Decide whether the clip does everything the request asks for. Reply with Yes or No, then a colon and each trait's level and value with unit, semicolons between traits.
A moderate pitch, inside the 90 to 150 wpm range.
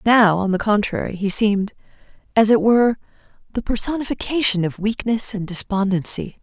No: high, 210 Hz; average, 140 wpm